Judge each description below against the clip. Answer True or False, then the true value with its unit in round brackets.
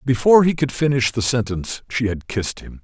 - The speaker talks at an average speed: False (210 wpm)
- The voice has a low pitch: True (125 Hz)